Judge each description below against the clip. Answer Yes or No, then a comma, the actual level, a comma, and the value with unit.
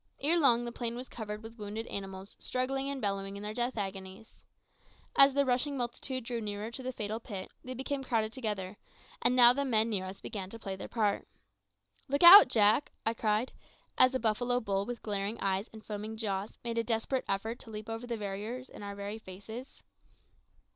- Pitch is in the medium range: No, high, 225 Hz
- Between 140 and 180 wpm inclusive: No, average, 200 wpm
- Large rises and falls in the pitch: No, average, 3.4 semitones